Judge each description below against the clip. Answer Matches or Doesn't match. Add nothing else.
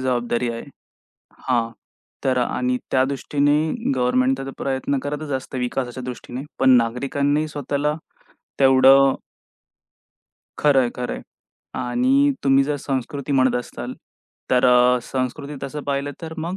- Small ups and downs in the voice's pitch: Matches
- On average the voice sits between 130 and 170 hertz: Matches